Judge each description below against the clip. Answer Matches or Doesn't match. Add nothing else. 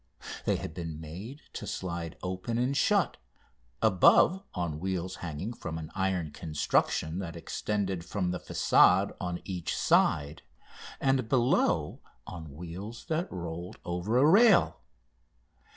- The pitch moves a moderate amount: Matches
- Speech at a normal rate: Doesn't match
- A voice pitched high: Doesn't match